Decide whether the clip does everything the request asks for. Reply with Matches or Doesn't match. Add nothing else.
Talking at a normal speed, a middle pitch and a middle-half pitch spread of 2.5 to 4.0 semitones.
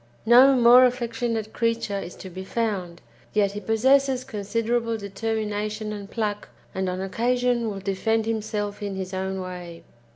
Doesn't match